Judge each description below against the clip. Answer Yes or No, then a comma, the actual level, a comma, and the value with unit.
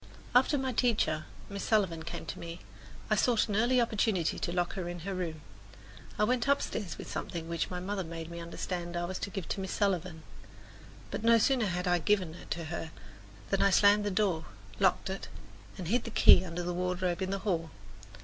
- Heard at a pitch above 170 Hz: Yes, medium, 185 Hz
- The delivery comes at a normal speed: No, fast, 210 wpm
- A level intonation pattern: No, average, 3.5 semitones